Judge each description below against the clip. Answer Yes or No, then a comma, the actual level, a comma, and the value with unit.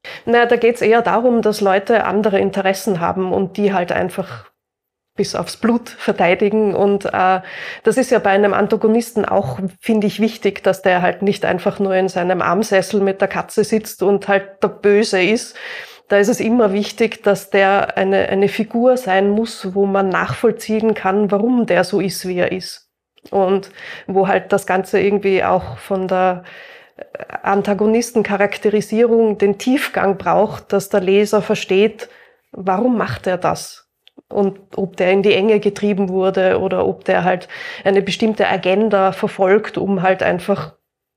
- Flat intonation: Yes, narrow, 2.2 semitones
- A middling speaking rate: Yes, average, 165 wpm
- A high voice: Yes, high, 200 Hz